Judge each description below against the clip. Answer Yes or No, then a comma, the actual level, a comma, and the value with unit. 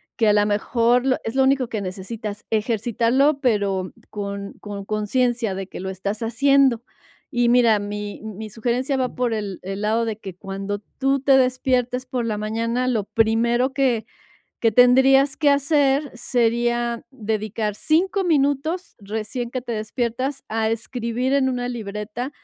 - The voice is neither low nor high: No, high, 235 Hz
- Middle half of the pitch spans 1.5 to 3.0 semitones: No, average, 3.5 semitones